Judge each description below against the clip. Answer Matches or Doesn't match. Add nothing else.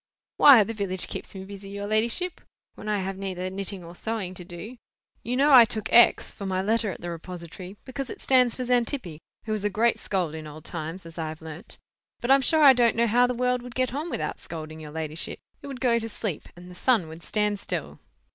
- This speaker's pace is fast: Matches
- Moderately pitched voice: Doesn't match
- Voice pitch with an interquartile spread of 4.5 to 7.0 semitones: Matches